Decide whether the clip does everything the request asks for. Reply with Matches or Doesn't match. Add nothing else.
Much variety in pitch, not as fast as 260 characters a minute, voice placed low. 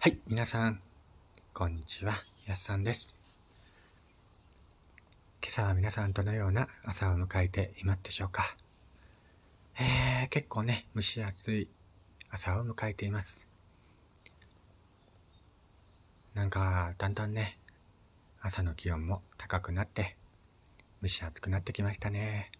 Doesn't match